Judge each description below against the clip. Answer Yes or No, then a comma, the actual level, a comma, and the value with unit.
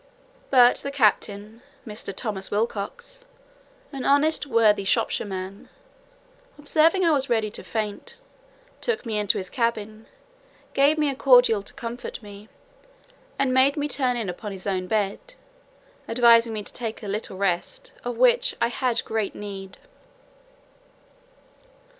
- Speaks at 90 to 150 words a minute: Yes, average, 140 wpm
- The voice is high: Yes, high, 230 Hz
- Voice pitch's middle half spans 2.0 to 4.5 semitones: No, average, 5.1 semitones